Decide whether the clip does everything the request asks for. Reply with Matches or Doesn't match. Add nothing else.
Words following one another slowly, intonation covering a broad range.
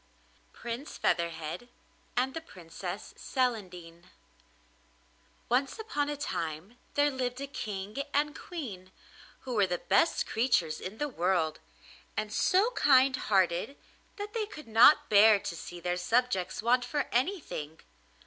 Matches